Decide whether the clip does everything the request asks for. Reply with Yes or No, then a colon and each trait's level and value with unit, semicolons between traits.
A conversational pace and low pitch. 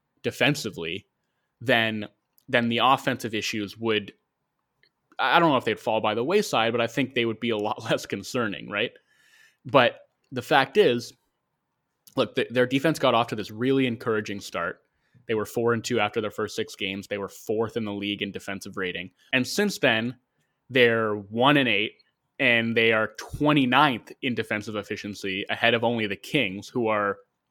Yes: average, 180 wpm; low, 115 Hz